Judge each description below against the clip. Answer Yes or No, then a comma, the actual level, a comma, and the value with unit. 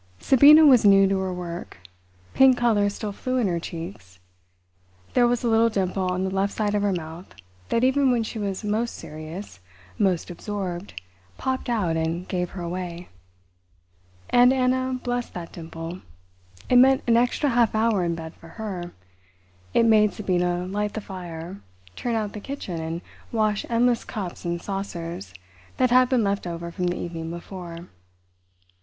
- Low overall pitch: No, high, 195 Hz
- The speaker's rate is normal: Yes, average, 165 wpm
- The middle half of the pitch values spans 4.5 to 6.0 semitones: Yes, average, 5.0 semitones